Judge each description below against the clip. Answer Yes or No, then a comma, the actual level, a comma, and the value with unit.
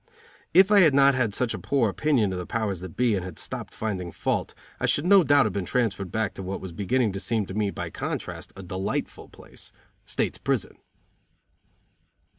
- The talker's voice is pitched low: Yes, low, 105 Hz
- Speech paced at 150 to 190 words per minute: No, fast, 205 wpm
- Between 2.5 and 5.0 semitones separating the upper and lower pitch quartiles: No, wide, 5.4 semitones